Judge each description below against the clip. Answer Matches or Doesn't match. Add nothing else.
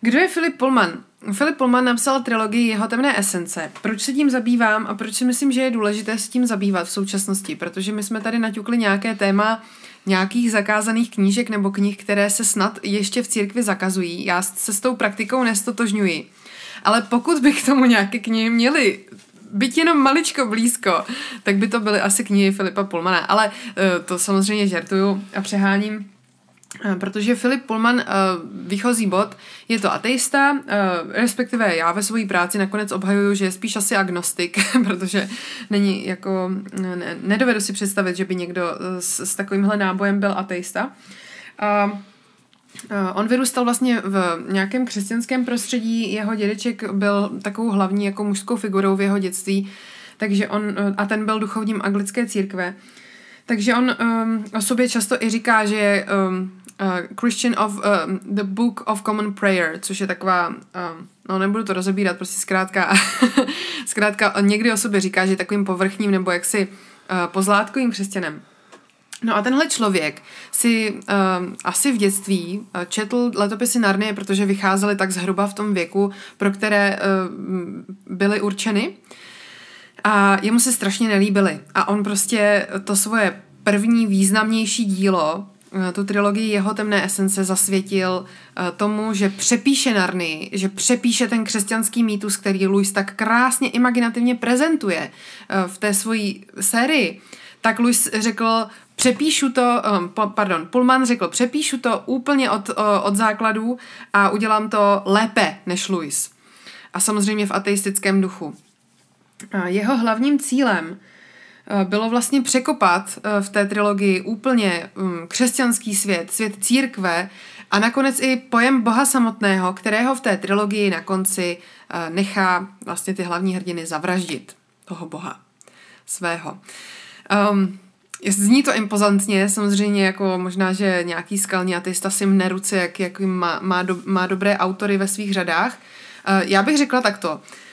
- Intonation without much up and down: Doesn't match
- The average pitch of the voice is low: Doesn't match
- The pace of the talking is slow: Doesn't match